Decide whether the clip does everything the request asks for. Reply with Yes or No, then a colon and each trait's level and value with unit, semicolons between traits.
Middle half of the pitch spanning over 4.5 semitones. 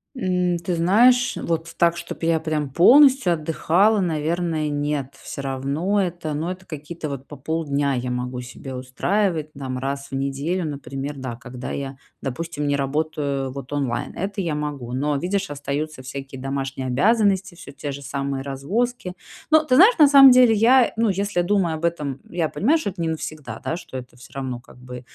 Yes: average, 5.0 semitones